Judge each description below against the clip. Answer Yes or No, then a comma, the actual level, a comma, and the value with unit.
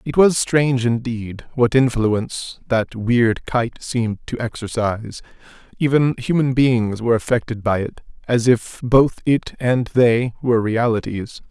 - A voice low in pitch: Yes, low, 120 Hz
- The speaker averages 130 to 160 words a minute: Yes, average, 140 wpm